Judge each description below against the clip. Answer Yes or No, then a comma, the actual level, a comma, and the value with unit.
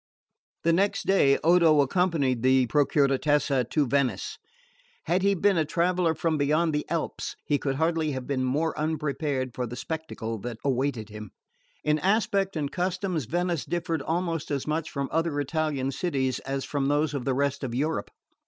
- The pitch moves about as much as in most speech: Yes, average, 3.6 semitones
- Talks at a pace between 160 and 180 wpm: Yes, average, 170 wpm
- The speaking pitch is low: No, medium, 150 Hz